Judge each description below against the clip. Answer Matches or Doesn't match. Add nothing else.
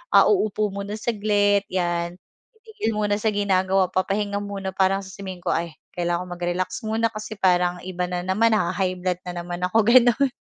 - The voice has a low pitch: Doesn't match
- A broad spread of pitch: Doesn't match